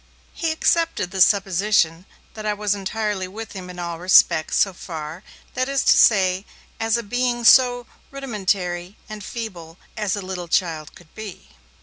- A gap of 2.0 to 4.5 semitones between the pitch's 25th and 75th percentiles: Yes, average, 3.9 semitones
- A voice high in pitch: Yes, high, 200 Hz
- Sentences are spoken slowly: No, average, 160 wpm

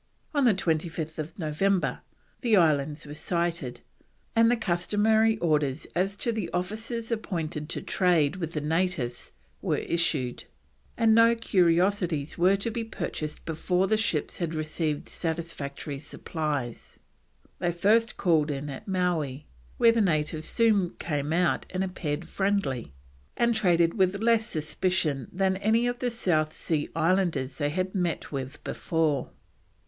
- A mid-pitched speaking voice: Yes, medium, 175 Hz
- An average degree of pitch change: Yes, average, 4.6 semitones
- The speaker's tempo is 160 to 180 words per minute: No, average, 140 wpm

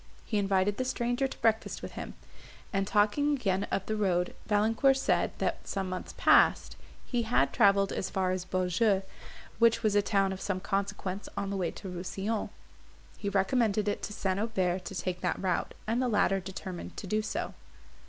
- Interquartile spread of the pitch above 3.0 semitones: No, narrow, 2.6 semitones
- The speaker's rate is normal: Yes, average, 185 wpm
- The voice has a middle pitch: No, high, 200 Hz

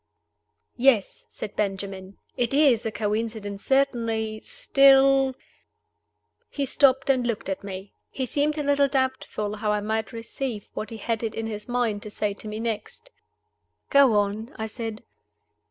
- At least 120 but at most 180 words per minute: Yes, average, 155 wpm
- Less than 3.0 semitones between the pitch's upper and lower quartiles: No, average, 4.2 semitones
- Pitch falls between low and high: No, high, 225 Hz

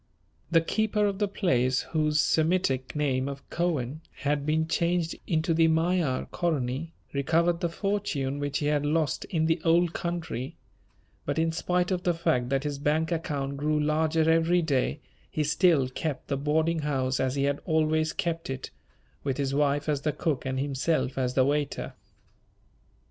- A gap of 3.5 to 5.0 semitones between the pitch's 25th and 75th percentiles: No, average, 3.1 semitones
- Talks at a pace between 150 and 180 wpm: Yes, average, 170 wpm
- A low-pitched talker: No, medium, 155 Hz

